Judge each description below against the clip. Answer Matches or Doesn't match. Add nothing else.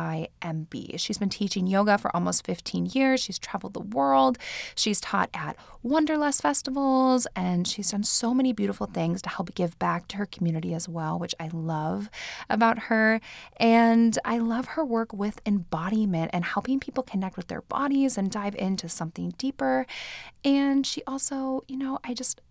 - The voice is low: Doesn't match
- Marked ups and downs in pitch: Matches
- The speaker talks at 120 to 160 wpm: Doesn't match